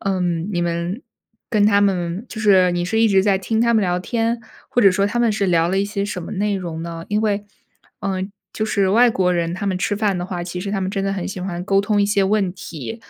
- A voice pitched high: Yes, high, 195 Hz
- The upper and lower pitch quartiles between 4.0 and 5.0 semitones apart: No, narrow, 2.6 semitones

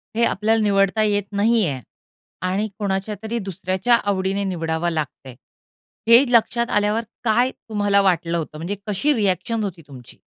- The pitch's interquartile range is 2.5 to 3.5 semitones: Yes, average, 3.1 semitones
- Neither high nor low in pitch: No, high, 200 Hz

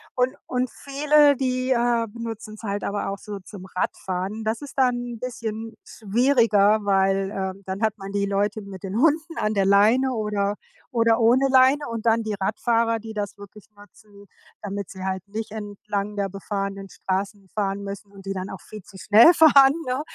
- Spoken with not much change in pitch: No, average, 3.0 semitones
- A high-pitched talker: Yes, high, 210 Hz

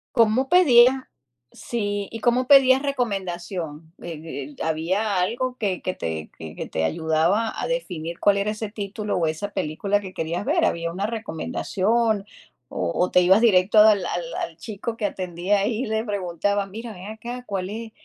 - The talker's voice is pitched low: No, high, 200 Hz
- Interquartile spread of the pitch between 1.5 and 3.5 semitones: No, average, 4.6 semitones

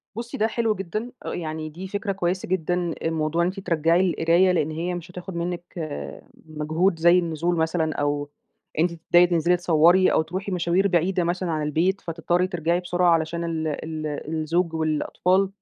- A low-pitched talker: No, medium, 170 Hz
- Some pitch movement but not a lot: No, narrow, 2.1 semitones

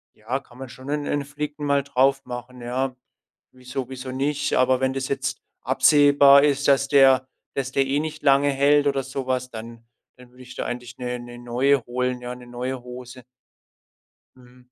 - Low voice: Yes, low, 130 Hz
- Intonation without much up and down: Yes, narrow, 1.9 semitones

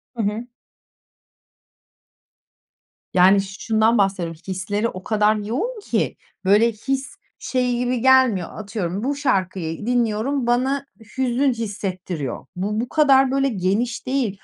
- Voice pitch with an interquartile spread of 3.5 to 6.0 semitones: Yes, average, 4.8 semitones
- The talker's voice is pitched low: No, high, 225 Hz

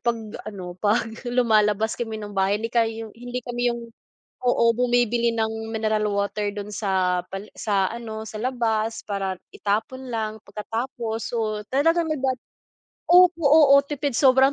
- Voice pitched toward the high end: Yes, high, 225 Hz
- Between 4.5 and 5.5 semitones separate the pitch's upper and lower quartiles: No, average, 2.9 semitones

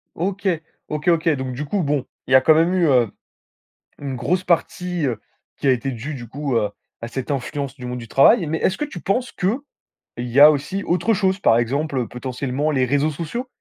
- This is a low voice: No, medium, 145 Hz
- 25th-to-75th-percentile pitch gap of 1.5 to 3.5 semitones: No, average, 5.3 semitones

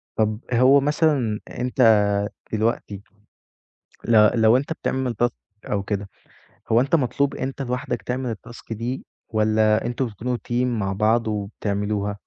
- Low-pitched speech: Yes, low, 115 Hz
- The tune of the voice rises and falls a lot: No, average, 2.9 semitones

